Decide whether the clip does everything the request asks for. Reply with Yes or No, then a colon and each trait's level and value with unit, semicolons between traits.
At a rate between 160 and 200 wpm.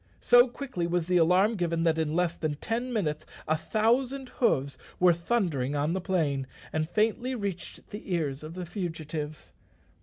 Yes: average, 170 wpm